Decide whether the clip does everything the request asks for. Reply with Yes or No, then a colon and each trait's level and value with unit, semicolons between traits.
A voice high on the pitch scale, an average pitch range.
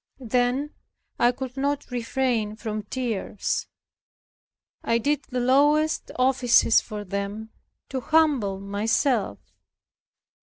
Yes: high, 245 Hz; average, 3.8 semitones